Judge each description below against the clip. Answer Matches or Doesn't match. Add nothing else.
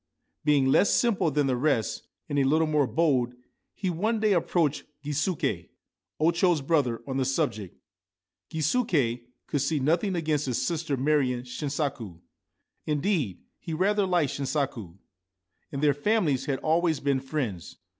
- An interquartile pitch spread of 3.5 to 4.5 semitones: Matches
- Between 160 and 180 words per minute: Doesn't match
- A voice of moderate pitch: Matches